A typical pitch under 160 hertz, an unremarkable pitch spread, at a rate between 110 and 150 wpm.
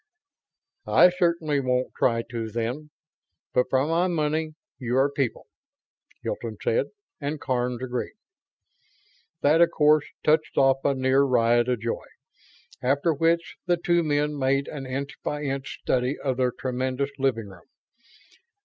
Yes: medium, 140 Hz; average, 3.4 semitones; average, 140 wpm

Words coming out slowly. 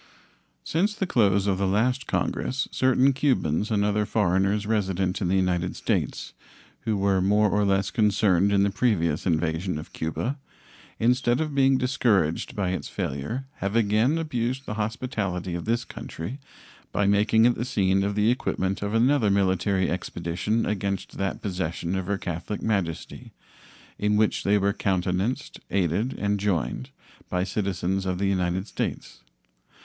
No: average, 155 wpm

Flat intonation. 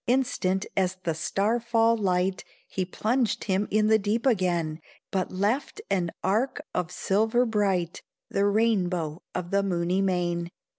No: average, 3.5 semitones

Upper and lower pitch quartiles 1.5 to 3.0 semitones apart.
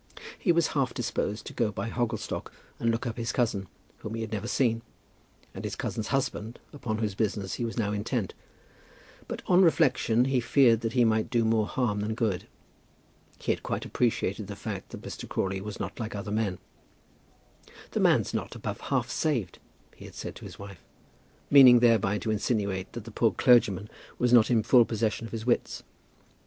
Yes: narrow, 2.6 semitones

